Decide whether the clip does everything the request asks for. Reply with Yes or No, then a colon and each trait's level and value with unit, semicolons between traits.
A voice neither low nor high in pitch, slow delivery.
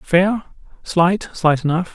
Yes: medium, 175 Hz; slow, 95 wpm